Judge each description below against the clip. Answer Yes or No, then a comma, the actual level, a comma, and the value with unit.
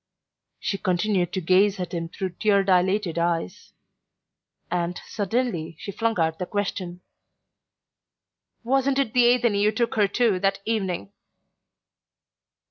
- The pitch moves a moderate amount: Yes, average, 3.7 semitones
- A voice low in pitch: No, high, 195 Hz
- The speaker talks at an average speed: No, slow, 125 wpm